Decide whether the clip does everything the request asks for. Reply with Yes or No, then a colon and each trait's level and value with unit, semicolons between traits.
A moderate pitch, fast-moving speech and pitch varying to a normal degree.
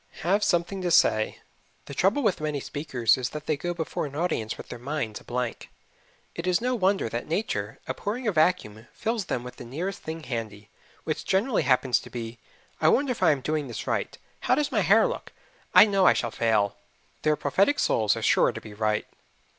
No: medium, 150 Hz; fast, 210 wpm; wide, 8.1 semitones